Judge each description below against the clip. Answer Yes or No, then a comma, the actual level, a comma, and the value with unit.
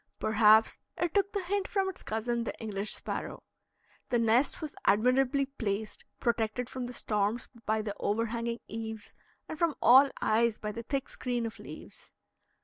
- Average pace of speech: Yes, average, 160 wpm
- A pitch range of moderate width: Yes, average, 3.7 semitones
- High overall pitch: Yes, high, 235 Hz